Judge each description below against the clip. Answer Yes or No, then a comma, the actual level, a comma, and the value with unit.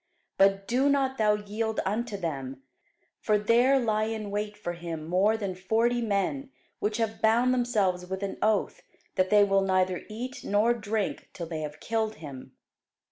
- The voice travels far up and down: No, average, 3.2 semitones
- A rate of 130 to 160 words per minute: No, average, 170 wpm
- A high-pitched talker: Yes, high, 210 Hz